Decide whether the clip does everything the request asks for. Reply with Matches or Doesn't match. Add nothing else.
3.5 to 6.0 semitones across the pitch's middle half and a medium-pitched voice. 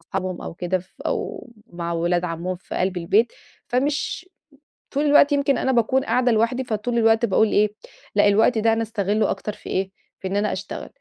Doesn't match